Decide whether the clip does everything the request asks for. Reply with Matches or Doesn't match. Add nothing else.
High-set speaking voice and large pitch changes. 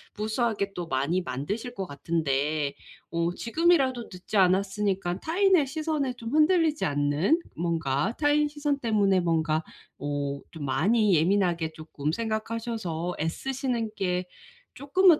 Matches